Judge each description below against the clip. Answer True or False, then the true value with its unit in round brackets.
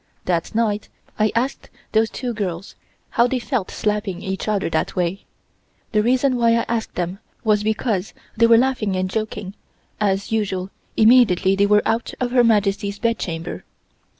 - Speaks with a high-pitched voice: True (210 Hz)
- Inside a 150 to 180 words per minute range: True (160 wpm)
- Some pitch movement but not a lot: True (3.2 semitones)